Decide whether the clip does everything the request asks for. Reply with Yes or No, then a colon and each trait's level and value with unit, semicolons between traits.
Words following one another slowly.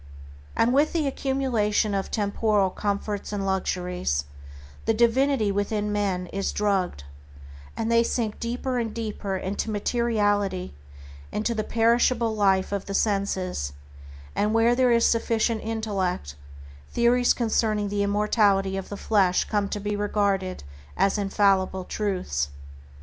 Yes: slow, 130 wpm